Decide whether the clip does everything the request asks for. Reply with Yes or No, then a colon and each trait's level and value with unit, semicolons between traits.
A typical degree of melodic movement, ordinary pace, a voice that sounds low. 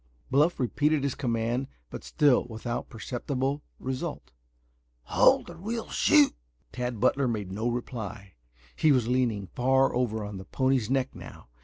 Yes: average, 3.4 semitones; average, 145 wpm; low, 125 Hz